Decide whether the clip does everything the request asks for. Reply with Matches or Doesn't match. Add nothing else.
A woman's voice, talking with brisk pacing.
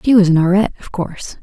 Matches